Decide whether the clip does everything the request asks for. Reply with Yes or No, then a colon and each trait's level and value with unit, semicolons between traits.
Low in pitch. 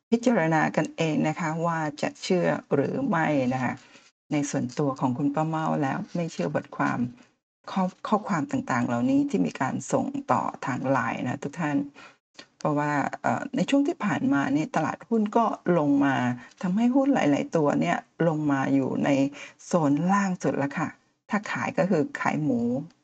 No: medium, 175 Hz